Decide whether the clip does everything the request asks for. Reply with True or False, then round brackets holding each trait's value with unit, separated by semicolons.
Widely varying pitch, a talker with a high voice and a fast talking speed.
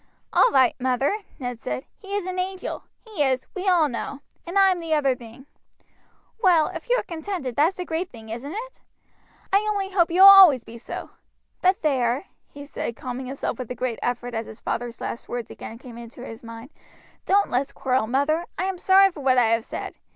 True (7.1 semitones; 280 Hz; 210 wpm)